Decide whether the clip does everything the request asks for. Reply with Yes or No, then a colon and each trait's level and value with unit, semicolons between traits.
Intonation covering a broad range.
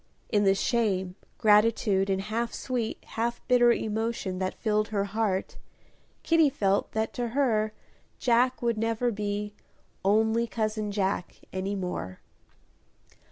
No: average, 2.8 semitones